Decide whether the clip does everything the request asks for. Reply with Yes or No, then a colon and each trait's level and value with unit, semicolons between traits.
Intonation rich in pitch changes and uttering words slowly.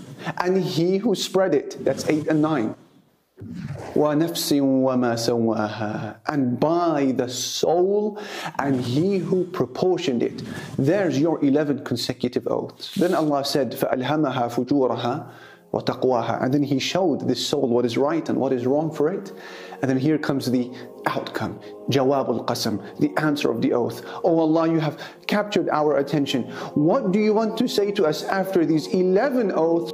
No: wide, 5.8 semitones; average, 145 wpm